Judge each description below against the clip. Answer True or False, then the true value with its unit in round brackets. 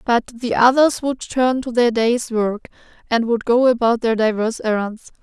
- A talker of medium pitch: False (235 Hz)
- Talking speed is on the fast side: False (185 wpm)